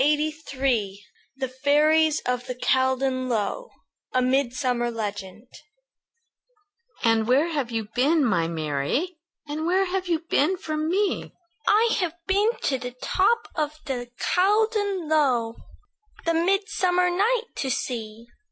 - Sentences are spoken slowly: Yes, slow, 125 wpm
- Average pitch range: No, wide, 6.5 semitones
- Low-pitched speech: No, very high, 290 Hz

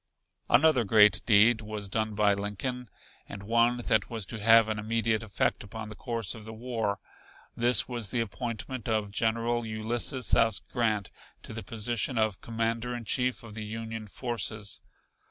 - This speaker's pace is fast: No, average, 165 wpm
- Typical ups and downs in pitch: No, narrow, 1.8 semitones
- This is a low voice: Yes, low, 110 Hz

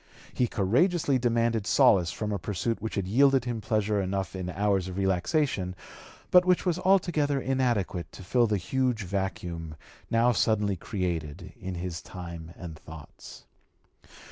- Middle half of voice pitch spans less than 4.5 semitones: No, average, 5.3 semitones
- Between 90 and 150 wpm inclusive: Yes, average, 145 wpm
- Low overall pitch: Yes, low, 100 Hz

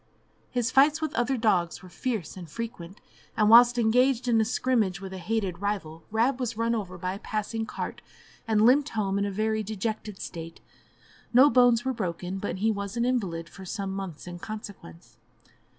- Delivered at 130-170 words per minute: No, average, 185 wpm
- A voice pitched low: No, high, 215 Hz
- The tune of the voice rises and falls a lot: No, average, 3.9 semitones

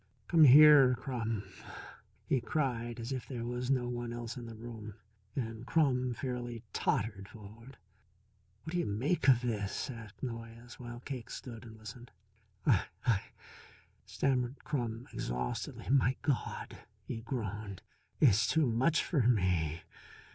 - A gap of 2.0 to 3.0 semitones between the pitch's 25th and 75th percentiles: Yes, narrow, 2.6 semitones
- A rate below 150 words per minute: Yes, average, 140 wpm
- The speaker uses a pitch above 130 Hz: No, low, 120 Hz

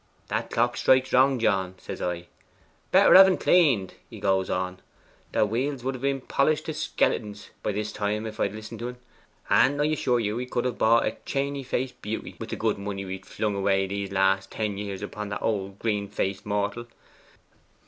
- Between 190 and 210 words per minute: Yes, average, 200 wpm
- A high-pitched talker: No, low, 105 Hz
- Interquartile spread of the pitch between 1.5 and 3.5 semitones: No, average, 4.2 semitones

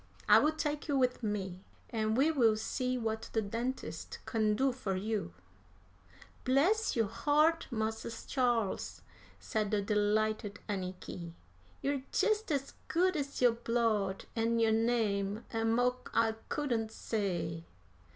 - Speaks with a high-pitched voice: Yes, high, 225 Hz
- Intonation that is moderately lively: Yes, average, 3.7 semitones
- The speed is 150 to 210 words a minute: No, slow, 135 wpm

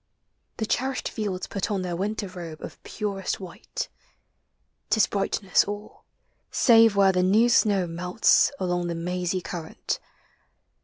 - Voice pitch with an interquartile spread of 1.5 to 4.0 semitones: Yes, average, 2.9 semitones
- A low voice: No, high, 190 Hz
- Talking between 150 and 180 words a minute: No, average, 140 wpm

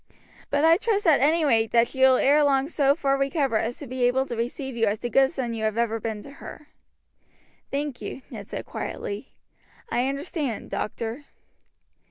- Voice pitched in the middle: No, very high, 270 Hz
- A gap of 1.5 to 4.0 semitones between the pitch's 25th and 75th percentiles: Yes, average, 3.7 semitones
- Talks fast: No, average, 195 wpm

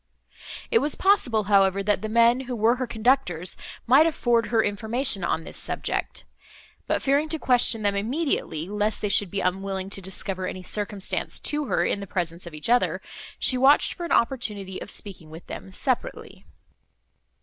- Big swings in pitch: No, average, 4.6 semitones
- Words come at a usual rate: Yes, average, 175 wpm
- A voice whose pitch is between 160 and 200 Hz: No, high, 210 Hz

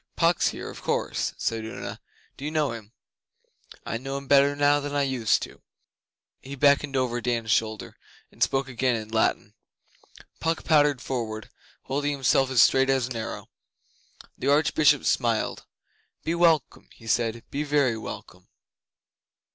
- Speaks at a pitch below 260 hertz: Yes, low, 135 Hz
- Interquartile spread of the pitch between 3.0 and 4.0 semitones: Yes, average, 3.6 semitones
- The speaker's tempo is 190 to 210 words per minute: No, average, 150 wpm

